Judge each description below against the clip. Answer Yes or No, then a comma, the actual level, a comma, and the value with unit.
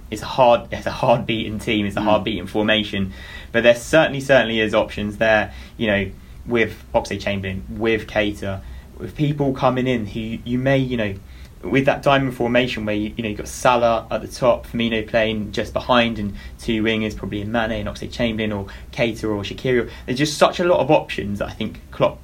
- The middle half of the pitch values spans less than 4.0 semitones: Yes, narrow, 2.6 semitones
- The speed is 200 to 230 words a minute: Yes, fast, 205 wpm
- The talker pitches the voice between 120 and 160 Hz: No, low, 110 Hz